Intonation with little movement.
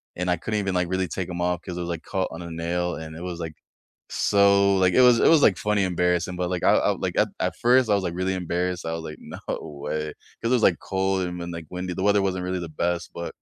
Yes: narrow, 1.9 semitones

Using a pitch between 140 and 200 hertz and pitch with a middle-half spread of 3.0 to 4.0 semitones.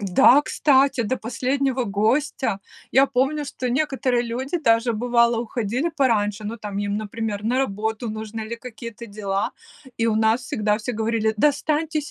No: high, 235 Hz; average, 3.6 semitones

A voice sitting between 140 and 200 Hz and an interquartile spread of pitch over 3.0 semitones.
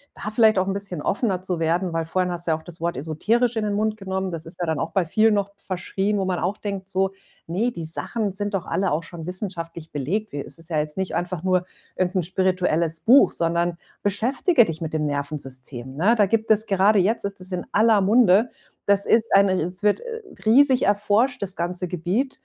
Yes: high, 190 Hz; average, 3.7 semitones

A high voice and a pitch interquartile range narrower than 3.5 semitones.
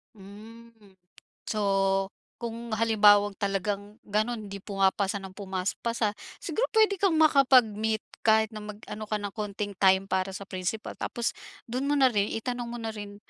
Yes: high, 215 Hz; narrow, 2.6 semitones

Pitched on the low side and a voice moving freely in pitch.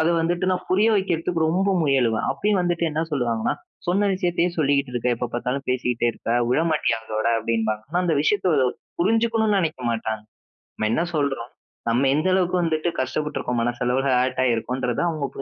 No: medium, 145 Hz; wide, 6.2 semitones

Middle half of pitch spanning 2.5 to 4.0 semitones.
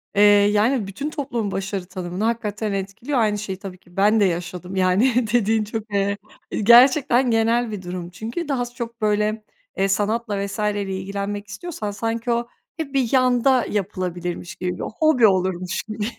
Yes: average, 3.4 semitones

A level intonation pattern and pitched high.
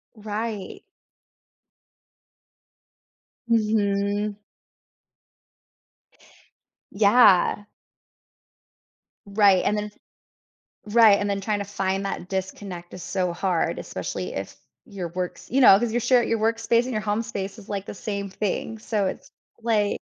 Yes: narrow, 2.0 semitones; high, 205 Hz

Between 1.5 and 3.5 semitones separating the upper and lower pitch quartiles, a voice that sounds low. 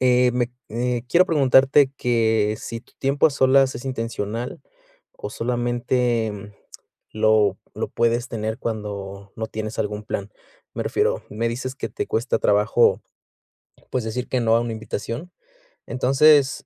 Yes: average, 2.8 semitones; low, 120 Hz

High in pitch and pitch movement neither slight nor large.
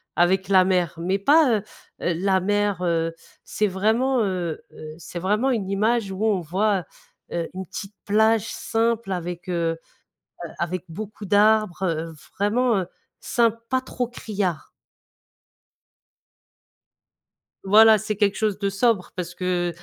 Yes: high, 195 Hz; average, 3.4 semitones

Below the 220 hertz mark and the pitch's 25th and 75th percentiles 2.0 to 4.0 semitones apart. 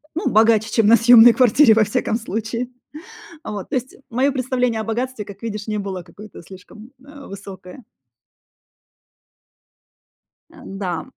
No: high, 225 Hz; average, 3.3 semitones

